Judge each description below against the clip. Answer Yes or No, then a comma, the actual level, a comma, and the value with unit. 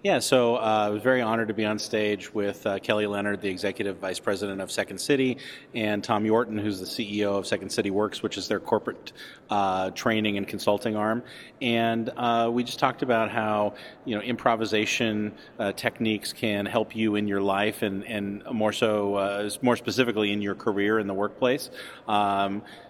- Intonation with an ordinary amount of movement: No, narrow, 2.1 semitones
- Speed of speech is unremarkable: Yes, average, 190 wpm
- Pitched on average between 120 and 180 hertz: No, low, 105 Hz